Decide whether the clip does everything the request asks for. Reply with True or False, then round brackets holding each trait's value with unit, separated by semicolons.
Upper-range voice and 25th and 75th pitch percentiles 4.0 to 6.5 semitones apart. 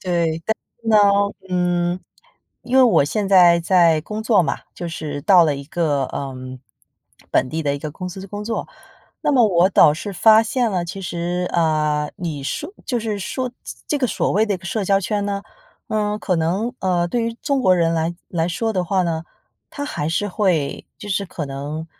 False (180 Hz; 4.3 semitones)